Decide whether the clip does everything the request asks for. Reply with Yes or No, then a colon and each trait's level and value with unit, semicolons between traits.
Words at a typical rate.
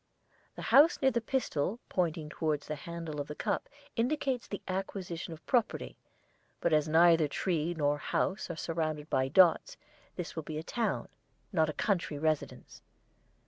Yes: average, 160 wpm